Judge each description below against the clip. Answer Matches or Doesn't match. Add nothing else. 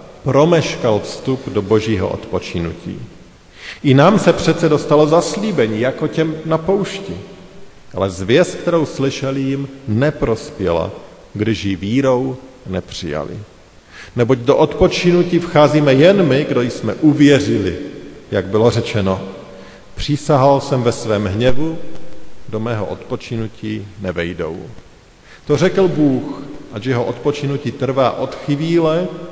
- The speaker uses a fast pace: Doesn't match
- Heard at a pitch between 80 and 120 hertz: Doesn't match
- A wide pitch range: Matches